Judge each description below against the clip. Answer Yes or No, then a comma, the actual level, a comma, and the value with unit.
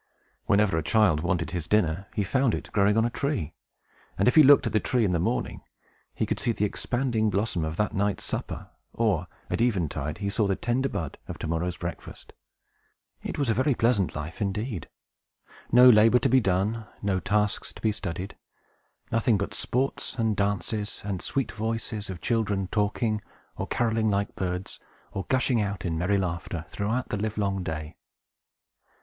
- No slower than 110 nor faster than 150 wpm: No, average, 180 wpm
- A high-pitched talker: No, low, 105 Hz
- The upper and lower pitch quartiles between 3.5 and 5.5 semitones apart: Yes, average, 3.8 semitones